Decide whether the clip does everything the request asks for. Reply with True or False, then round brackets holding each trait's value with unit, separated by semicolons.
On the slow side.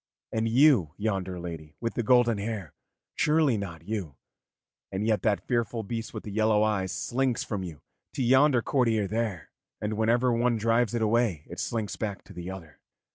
False (180 wpm)